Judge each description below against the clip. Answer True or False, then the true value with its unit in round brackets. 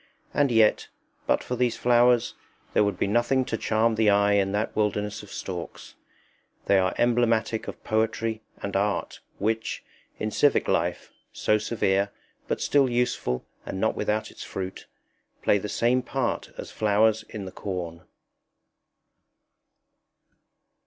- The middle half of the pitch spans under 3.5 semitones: True (2.7 semitones)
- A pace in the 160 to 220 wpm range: False (140 wpm)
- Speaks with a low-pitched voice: True (110 Hz)